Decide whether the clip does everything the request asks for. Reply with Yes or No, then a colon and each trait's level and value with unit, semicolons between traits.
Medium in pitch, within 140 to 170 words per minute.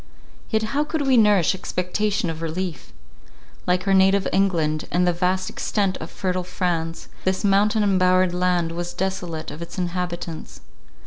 Yes: medium, 180 Hz; average, 150 wpm